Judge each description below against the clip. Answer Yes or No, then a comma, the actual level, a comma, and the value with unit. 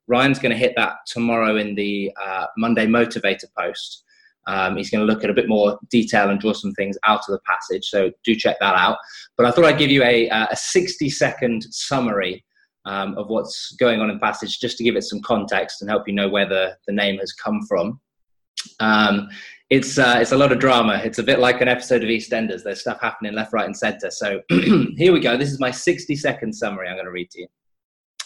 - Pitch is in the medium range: No, low, 115 Hz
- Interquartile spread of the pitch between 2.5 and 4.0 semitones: Yes, average, 3.5 semitones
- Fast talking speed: Yes, fast, 225 wpm